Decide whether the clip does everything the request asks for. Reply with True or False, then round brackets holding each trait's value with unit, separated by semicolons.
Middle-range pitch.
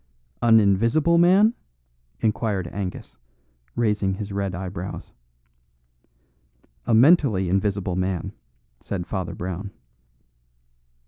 False (100 Hz)